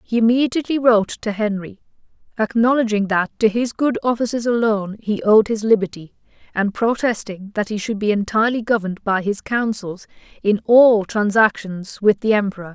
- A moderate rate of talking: Yes, average, 155 wpm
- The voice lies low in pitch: No, high, 215 Hz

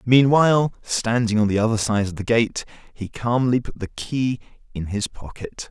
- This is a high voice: No, low, 115 Hz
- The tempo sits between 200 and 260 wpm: No, average, 180 wpm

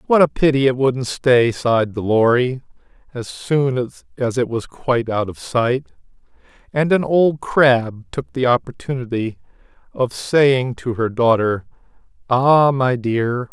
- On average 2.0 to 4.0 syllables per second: Yes, 3.9 syllables/s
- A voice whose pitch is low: Yes, low, 125 Hz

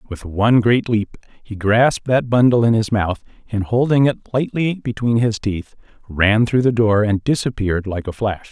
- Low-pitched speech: Yes, low, 110 Hz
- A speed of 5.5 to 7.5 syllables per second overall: No, 4.9 syllables/s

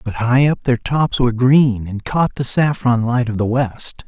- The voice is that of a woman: No, male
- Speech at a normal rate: No, fast, 220 wpm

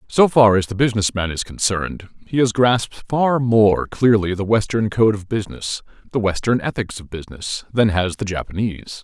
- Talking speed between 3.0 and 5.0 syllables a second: No, 5.3 syllables/s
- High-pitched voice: No, low, 105 Hz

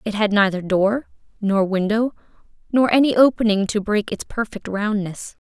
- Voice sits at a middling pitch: No, high, 210 Hz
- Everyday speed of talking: Yes, average, 155 wpm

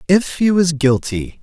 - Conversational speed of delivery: Yes, average, 170 wpm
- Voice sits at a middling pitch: Yes, medium, 165 Hz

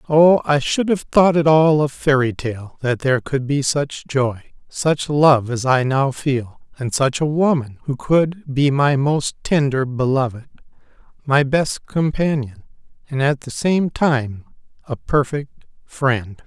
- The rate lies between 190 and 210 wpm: No, average, 160 wpm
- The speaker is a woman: No, male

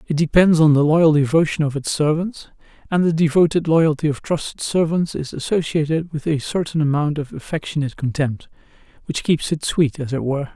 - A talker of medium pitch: Yes, medium, 155 Hz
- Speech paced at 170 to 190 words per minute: Yes, average, 180 wpm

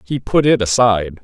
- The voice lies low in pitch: Yes, low, 110 Hz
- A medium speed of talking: Yes, average, 195 wpm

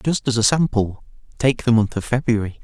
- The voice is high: No, low, 120 Hz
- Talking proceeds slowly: No, fast, 205 wpm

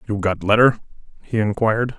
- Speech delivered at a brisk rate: No, average, 150 wpm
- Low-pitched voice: Yes, low, 110 Hz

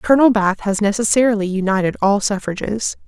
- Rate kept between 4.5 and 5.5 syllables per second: No, 5.8 syllables/s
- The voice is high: Yes, high, 210 Hz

